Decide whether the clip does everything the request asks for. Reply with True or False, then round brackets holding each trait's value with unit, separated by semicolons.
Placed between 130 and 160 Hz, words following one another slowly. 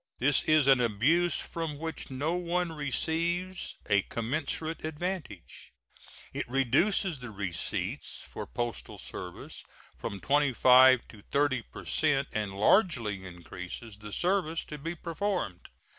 True (140 Hz; 125 wpm)